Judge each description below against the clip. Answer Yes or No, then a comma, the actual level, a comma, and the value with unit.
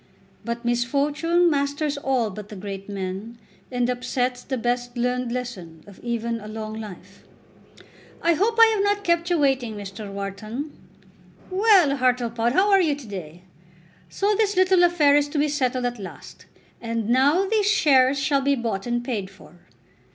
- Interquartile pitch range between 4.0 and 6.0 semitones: Yes, average, 5.1 semitones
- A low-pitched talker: No, very high, 250 Hz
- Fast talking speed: No, average, 165 wpm